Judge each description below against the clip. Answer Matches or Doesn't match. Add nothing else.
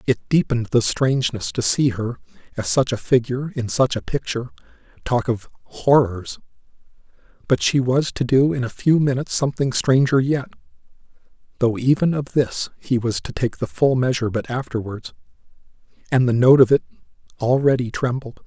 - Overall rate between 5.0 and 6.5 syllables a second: Matches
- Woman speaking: Doesn't match